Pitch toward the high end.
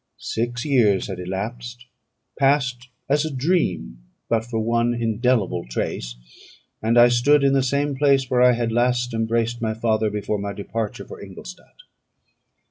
No: low, 120 Hz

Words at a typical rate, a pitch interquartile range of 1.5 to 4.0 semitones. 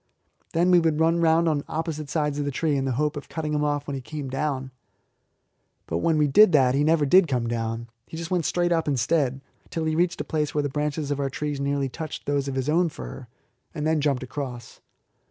No: fast, 230 wpm; average, 2.8 semitones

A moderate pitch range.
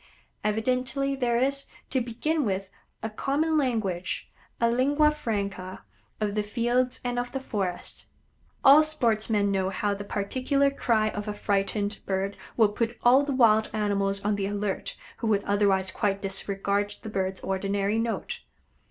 Yes: average, 4.0 semitones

